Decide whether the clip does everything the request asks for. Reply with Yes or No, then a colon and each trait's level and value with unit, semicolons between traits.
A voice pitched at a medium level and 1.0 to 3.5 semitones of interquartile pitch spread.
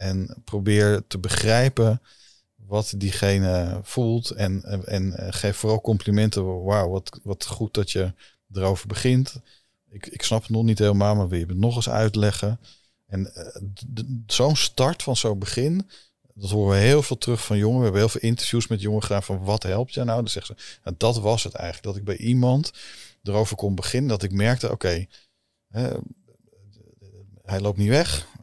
No: low, 105 Hz; average, 2.8 semitones